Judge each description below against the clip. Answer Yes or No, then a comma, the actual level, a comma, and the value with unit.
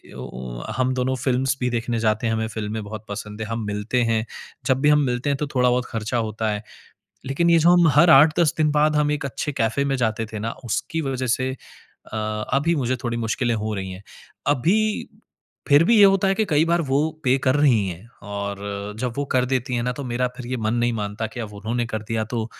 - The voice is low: Yes, low, 125 Hz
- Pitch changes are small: No, average, 4.2 semitones